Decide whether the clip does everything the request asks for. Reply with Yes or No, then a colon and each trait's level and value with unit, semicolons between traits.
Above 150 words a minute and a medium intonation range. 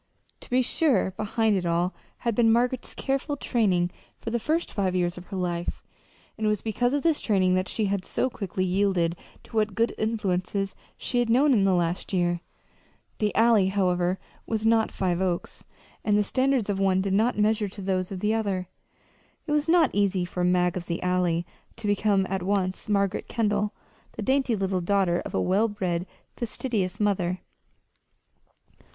Yes: average, 180 wpm; average, 3.6 semitones